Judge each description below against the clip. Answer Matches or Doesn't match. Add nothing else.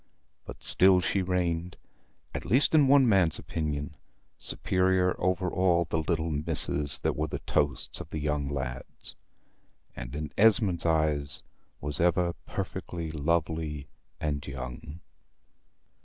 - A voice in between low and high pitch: Doesn't match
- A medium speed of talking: Doesn't match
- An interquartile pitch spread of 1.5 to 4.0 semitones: Matches